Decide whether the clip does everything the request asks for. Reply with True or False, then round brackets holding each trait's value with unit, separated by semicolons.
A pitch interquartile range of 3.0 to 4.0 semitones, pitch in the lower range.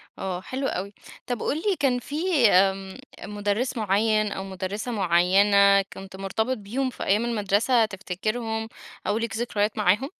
False (3.5 semitones; 210 Hz)